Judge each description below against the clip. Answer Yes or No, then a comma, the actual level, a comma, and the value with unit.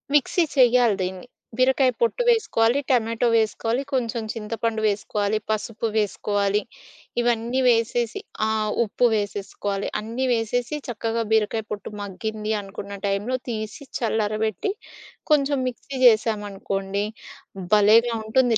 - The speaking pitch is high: Yes, high, 225 Hz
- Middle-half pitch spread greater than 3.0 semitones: No, narrow, 2.6 semitones